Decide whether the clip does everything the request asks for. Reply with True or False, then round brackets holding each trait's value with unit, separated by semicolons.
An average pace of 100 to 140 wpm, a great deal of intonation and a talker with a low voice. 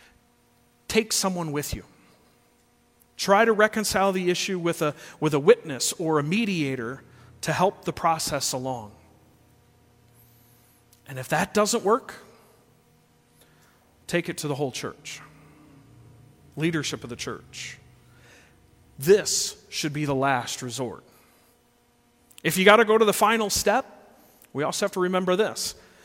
False (135 wpm; 7.2 semitones; 155 Hz)